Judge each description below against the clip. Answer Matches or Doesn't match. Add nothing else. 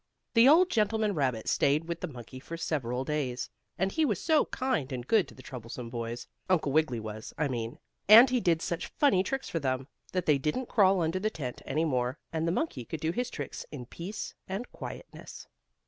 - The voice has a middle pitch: Matches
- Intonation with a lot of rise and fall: Matches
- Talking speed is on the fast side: Matches